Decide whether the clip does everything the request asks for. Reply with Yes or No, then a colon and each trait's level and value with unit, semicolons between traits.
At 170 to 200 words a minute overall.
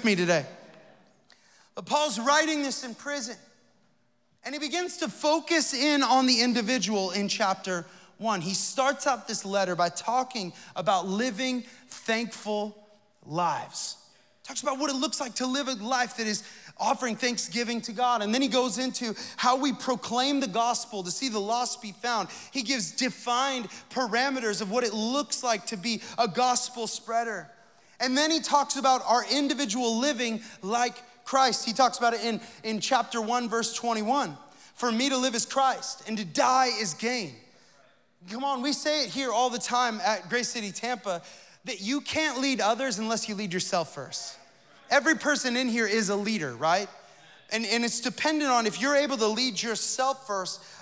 Yes: average, 180 wpm